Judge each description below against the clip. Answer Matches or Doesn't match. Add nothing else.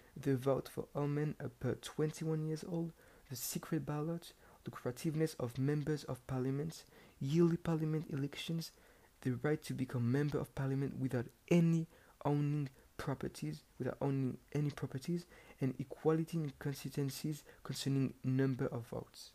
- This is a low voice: Doesn't match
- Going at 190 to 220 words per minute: Doesn't match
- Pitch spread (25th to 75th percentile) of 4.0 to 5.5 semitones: Doesn't match